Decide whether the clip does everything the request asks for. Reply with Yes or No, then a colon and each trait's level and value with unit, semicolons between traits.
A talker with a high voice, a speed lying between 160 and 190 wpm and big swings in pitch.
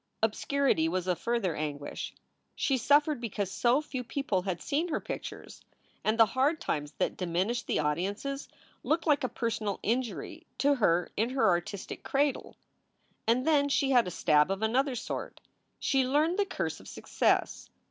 Yes: high, 235 Hz; average, 165 wpm; wide, 7.0 semitones